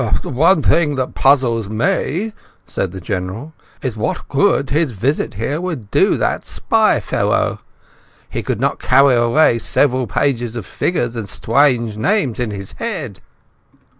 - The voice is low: Yes, low, 125 Hz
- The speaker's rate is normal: Yes, average, 150 wpm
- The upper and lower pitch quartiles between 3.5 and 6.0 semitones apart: Yes, average, 4.8 semitones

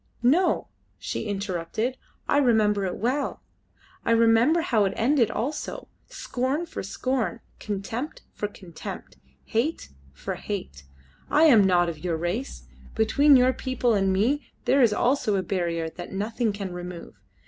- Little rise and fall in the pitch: No, average, 5.3 semitones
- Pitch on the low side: No, high, 220 Hz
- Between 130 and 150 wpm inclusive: Yes, average, 145 wpm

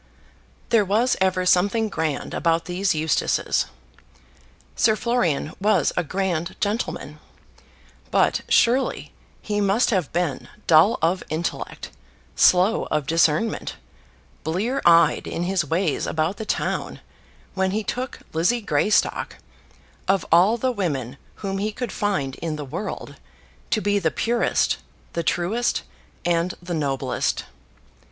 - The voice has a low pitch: No, medium, 185 Hz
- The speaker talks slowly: Yes, slow, 125 wpm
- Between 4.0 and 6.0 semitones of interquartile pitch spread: Yes, average, 4.4 semitones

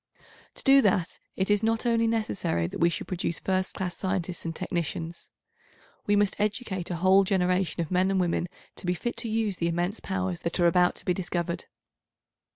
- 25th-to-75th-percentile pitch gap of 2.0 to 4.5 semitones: Yes, average, 2.9 semitones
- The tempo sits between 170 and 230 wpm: Yes, average, 195 wpm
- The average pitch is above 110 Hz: Yes, medium, 185 Hz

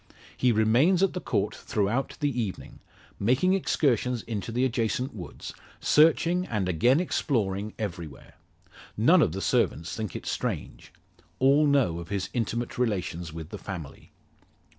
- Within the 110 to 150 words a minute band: Yes, average, 140 wpm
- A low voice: Yes, low, 115 Hz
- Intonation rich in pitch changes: Yes, wide, 6.0 semitones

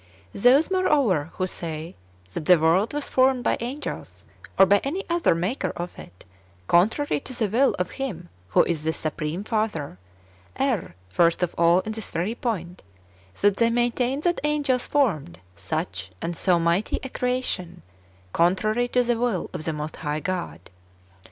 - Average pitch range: No, wide, 6.9 semitones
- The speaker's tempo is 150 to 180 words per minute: Yes, average, 165 wpm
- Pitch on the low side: No, high, 195 Hz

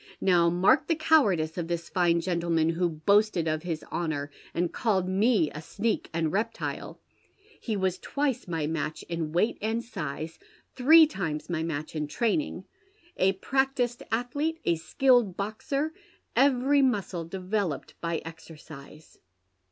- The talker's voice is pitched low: No, medium, 185 Hz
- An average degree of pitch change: No, wide, 6.4 semitones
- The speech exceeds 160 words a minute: No, average, 140 wpm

